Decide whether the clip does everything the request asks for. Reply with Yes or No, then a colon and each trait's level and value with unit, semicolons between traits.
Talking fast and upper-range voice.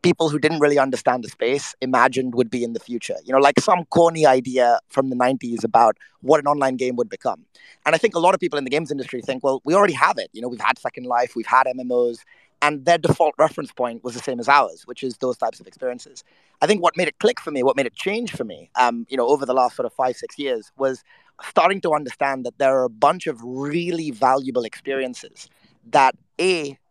No: fast, 250 wpm; low, 135 Hz